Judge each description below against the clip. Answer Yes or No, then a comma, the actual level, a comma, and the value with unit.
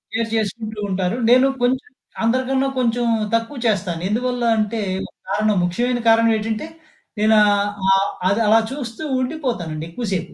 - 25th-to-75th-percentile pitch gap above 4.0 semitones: No, average, 3.3 semitones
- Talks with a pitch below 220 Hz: No, high, 225 Hz